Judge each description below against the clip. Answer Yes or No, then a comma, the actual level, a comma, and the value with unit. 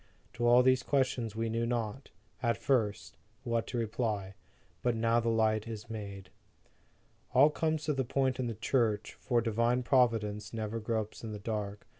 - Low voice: Yes, low, 115 Hz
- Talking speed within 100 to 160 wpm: No, average, 170 wpm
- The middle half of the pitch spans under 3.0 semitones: Yes, narrow, 2.4 semitones